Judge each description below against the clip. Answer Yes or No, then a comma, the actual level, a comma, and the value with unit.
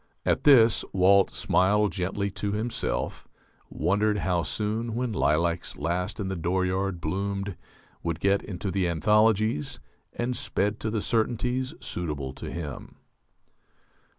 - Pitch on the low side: Yes, low, 100 Hz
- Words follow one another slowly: Yes, slow, 125 wpm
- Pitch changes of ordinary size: Yes, average, 3.6 semitones